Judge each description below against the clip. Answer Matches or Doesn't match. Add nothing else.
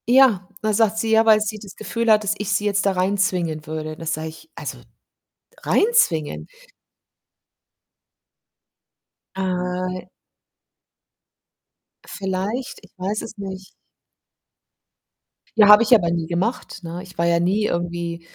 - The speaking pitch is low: Doesn't match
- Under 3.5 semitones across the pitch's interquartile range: Doesn't match